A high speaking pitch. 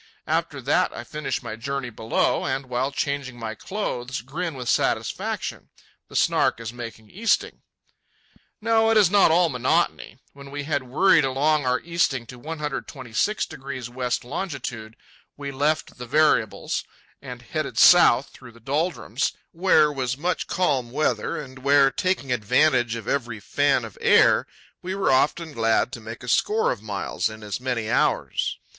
No: low, 135 Hz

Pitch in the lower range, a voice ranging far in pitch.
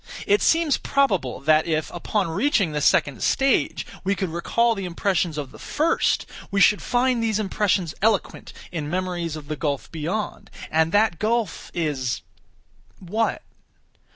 No: medium, 185 Hz; wide, 5.8 semitones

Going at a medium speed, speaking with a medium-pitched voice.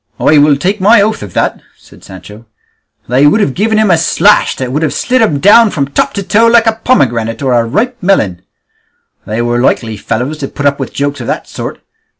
No: fast, 220 wpm; medium, 145 Hz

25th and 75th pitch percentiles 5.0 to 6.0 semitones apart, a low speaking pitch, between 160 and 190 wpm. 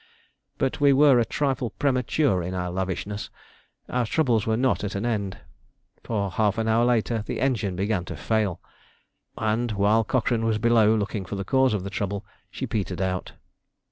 No: average, 3.5 semitones; low, 110 Hz; average, 175 wpm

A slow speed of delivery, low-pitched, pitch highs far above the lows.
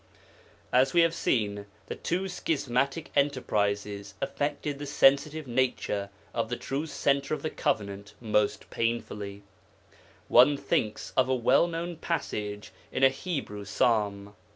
Yes: slow, 130 wpm; low, 130 Hz; wide, 5.8 semitones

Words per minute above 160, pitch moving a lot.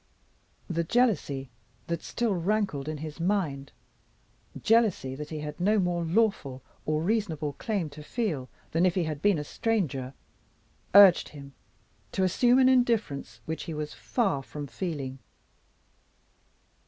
No: average, 140 wpm; wide, 6.0 semitones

